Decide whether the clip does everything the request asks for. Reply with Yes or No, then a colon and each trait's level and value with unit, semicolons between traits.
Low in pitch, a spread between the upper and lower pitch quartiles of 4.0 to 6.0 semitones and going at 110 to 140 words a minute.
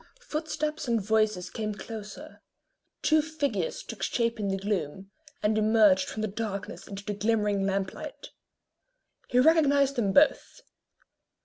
No: high, 215 Hz; wide, 5.6 semitones; slow, 135 wpm